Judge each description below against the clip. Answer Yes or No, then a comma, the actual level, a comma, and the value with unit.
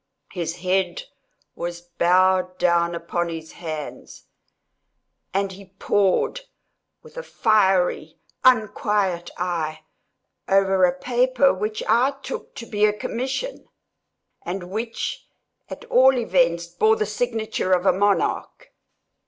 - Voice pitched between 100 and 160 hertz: No, high, 190 Hz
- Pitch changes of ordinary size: Yes, average, 4.1 semitones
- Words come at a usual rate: No, slow, 115 wpm